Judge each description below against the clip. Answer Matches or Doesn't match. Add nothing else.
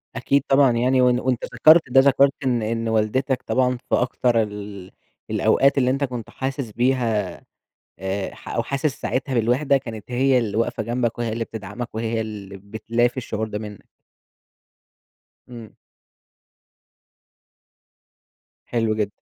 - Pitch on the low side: Matches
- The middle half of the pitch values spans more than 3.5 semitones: Doesn't match